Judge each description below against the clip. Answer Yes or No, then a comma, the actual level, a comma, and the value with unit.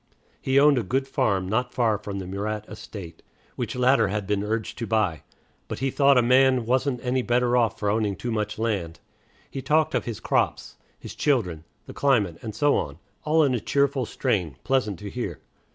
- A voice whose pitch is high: No, low, 115 Hz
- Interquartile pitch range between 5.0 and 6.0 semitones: No, average, 4.5 semitones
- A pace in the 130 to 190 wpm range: No, average, 200 wpm